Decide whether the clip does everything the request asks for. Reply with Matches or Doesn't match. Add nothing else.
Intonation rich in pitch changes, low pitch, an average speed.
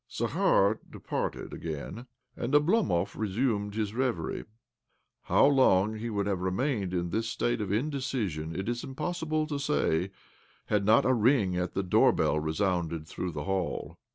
Matches